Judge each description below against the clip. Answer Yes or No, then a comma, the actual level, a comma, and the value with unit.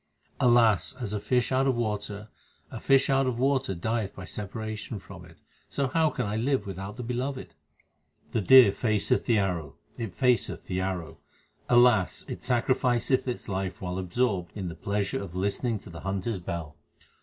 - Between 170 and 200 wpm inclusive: Yes, average, 180 wpm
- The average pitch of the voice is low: Yes, low, 105 Hz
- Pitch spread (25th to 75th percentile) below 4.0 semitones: No, average, 4.6 semitones